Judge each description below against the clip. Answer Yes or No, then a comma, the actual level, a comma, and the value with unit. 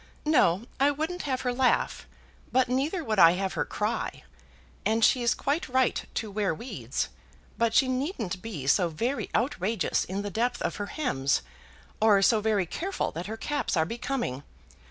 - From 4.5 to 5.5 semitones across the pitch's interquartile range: Yes, average, 5.1 semitones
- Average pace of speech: Yes, average, 170 wpm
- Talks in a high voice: Yes, high, 225 Hz